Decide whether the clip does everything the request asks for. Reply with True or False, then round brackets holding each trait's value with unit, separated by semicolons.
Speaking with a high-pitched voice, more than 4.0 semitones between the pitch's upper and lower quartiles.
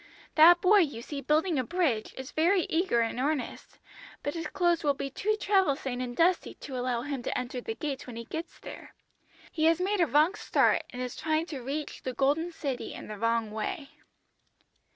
True (290 Hz; 5.1 semitones)